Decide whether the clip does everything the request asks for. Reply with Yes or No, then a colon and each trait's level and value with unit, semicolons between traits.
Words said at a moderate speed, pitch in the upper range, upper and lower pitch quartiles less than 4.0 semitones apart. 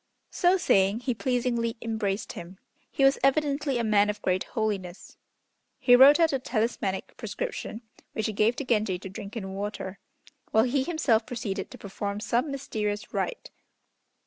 No: average, 160 wpm; high, 225 Hz; average, 4.5 semitones